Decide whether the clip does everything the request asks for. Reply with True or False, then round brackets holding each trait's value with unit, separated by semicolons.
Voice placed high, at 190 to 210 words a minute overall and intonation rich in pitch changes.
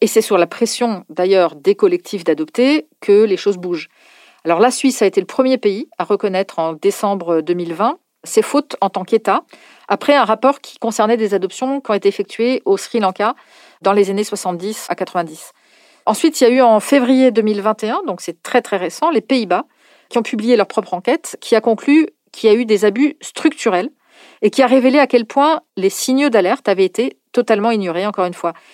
True (225 Hz; 205 wpm; 5.7 semitones)